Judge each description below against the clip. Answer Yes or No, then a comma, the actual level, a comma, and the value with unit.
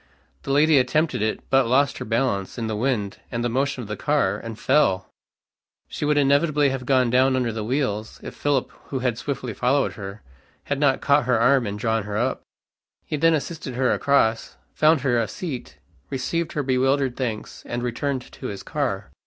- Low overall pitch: Yes, low, 130 Hz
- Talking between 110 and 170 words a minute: No, average, 195 wpm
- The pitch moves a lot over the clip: No, average, 3.7 semitones